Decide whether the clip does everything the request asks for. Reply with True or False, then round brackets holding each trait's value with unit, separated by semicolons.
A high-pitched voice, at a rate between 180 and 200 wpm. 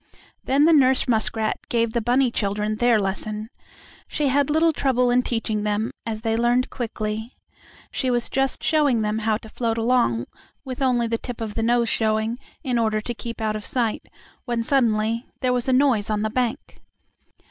True (230 Hz; 185 wpm)